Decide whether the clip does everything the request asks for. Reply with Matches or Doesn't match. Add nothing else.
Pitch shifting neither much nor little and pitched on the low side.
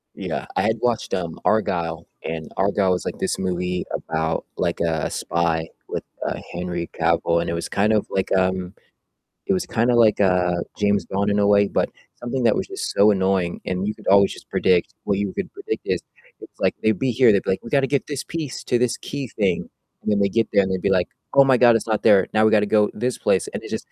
Matches